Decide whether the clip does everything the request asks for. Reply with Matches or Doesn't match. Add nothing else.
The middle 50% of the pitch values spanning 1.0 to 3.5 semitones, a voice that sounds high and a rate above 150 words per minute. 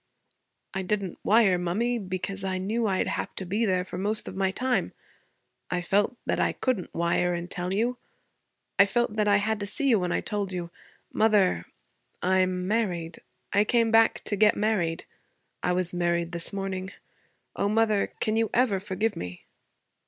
Matches